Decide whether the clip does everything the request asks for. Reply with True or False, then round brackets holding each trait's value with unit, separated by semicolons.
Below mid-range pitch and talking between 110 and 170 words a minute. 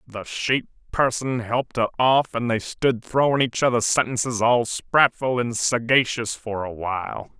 True (120 Hz; 160 wpm)